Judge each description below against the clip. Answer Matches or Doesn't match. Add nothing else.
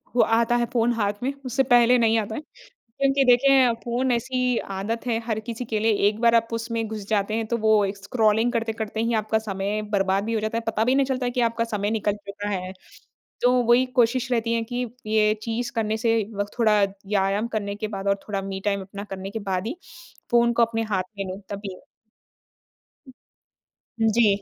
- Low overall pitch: Doesn't match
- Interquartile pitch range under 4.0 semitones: Matches